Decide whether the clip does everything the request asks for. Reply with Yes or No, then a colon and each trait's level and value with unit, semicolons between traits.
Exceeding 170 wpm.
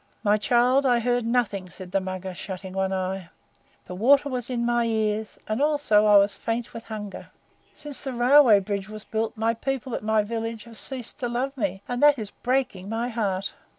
Yes: average, 200 wpm